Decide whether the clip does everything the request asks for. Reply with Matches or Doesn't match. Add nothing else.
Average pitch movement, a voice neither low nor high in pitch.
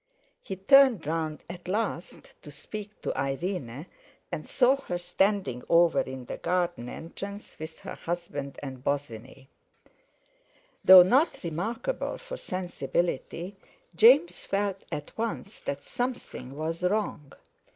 Doesn't match